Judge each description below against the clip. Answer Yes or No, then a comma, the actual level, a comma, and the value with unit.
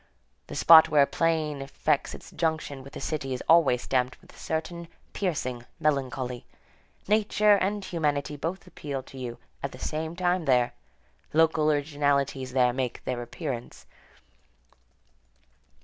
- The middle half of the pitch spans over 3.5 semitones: Yes, average, 4.0 semitones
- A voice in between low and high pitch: Yes, medium, 145 Hz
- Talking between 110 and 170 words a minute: Yes, average, 140 wpm